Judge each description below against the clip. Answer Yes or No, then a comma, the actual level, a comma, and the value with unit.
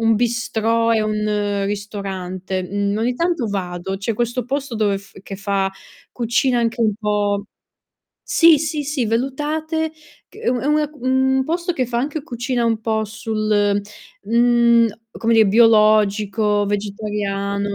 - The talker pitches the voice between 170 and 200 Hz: No, high, 220 Hz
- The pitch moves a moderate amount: Yes, average, 3.2 semitones